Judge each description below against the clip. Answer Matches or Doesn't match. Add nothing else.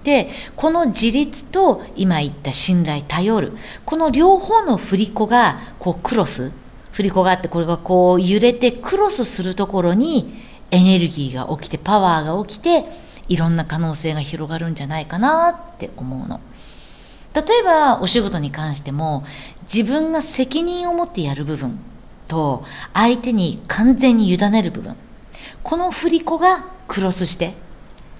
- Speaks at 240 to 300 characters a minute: Matches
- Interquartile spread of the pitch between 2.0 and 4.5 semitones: Doesn't match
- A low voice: Doesn't match